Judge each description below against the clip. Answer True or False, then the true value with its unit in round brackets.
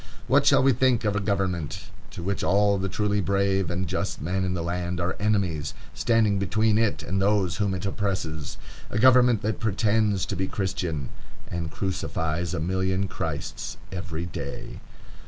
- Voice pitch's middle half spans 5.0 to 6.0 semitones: False (2.8 semitones)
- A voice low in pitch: True (95 Hz)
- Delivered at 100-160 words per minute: False (170 wpm)